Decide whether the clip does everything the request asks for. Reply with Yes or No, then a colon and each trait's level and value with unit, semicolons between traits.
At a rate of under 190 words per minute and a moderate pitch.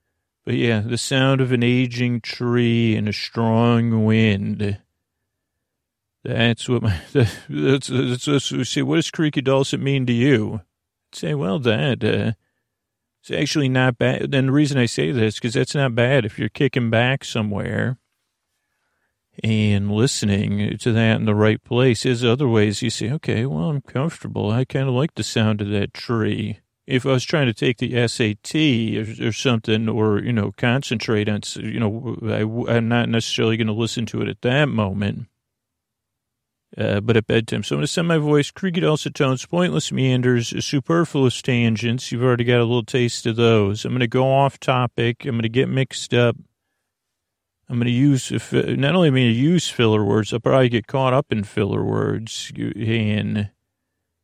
No: average, 175 wpm; low, 120 Hz